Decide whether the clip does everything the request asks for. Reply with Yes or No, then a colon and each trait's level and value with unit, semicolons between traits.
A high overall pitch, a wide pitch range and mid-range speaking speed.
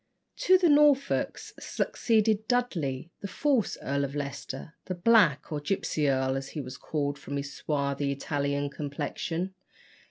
No: medium, 145 Hz; wide, 6.6 semitones; average, 145 wpm